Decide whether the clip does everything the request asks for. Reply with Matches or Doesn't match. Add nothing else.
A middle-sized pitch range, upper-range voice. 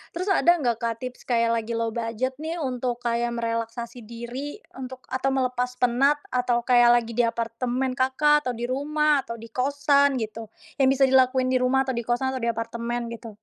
Doesn't match